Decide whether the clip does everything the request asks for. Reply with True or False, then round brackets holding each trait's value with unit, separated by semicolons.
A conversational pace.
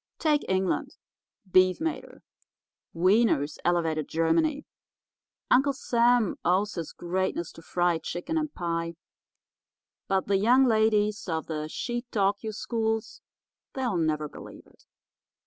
False (115 wpm)